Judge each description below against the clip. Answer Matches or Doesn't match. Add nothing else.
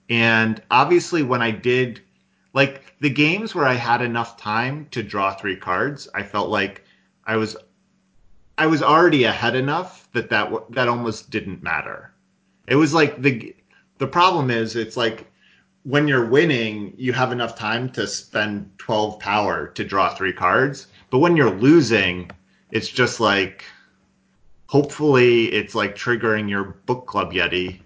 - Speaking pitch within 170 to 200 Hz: Doesn't match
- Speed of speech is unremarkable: Matches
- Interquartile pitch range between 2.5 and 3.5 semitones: Doesn't match